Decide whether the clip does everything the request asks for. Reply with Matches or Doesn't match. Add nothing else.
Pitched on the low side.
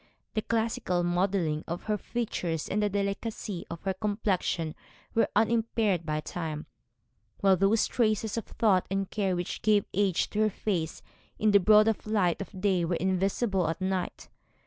Doesn't match